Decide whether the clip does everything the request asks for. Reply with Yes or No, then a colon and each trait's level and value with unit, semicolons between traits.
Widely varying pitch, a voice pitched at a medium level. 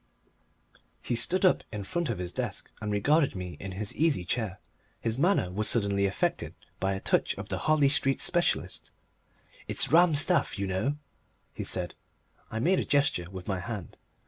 No: wide, 7.4 semitones; low, 110 Hz